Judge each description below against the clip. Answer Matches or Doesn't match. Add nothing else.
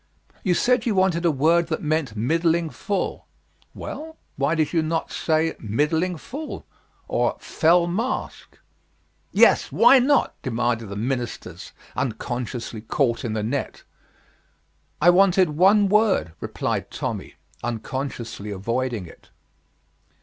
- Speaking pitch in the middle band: Matches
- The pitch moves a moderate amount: Doesn't match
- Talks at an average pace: Doesn't match